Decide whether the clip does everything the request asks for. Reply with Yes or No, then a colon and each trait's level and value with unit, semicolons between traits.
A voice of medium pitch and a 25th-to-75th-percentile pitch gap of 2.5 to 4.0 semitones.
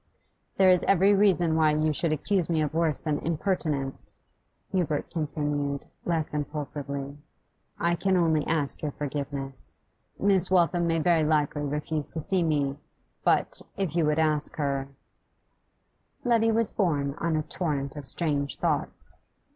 Yes: medium, 155 Hz; average, 3.0 semitones